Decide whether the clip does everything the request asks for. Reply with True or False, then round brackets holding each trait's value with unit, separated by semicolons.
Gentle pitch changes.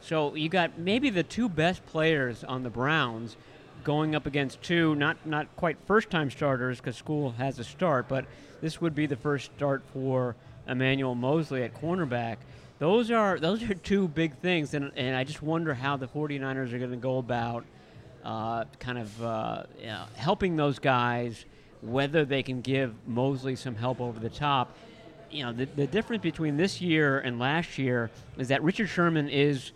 False (4.1 semitones)